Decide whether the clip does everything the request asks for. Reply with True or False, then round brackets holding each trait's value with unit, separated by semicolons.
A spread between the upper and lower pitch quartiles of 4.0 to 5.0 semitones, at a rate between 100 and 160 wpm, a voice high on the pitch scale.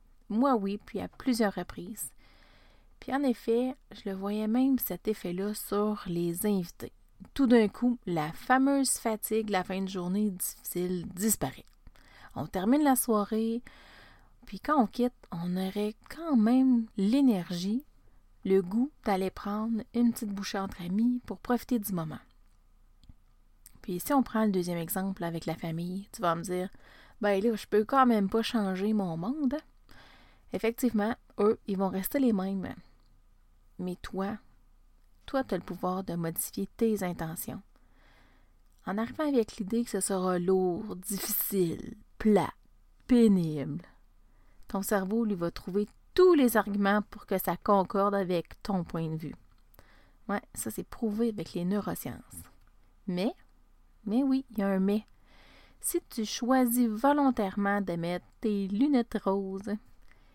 True (4.3 semitones; 150 wpm; 205 Hz)